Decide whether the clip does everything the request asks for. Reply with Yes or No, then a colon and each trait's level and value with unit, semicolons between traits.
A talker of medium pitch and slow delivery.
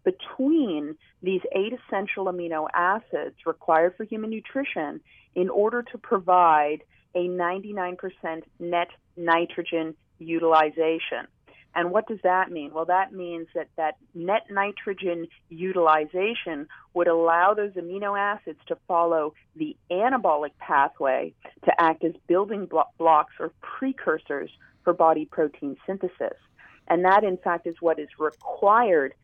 Yes: medium, 175 Hz; slow, 125 wpm